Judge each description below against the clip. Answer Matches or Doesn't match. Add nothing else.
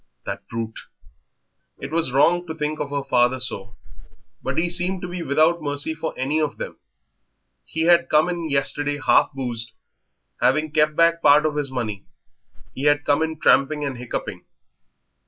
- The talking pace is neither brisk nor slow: Matches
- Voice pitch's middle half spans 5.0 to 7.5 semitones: Doesn't match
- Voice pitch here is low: Doesn't match